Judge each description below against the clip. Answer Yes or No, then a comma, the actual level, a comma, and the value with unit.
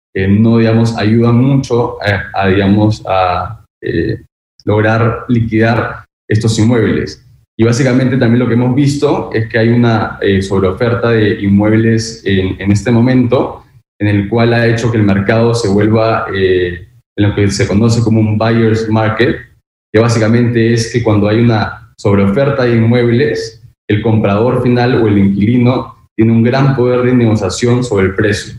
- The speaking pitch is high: No, low, 115 Hz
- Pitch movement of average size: No, narrow, 2.3 semitones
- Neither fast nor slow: Yes, average, 165 wpm